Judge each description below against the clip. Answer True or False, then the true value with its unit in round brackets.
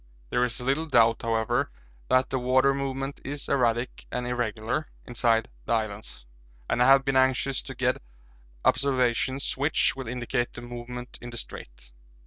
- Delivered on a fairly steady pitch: True (2.2 semitones)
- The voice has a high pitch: False (125 Hz)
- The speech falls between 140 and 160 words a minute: True (155 wpm)